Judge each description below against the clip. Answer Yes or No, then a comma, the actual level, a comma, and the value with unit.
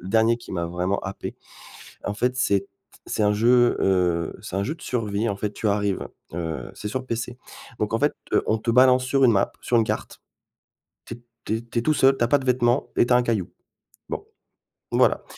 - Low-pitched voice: Yes, low, 115 Hz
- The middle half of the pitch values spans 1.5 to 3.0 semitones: No, average, 3.6 semitones